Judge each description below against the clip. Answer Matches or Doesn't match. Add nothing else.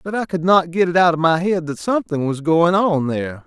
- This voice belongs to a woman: Doesn't match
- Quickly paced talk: Matches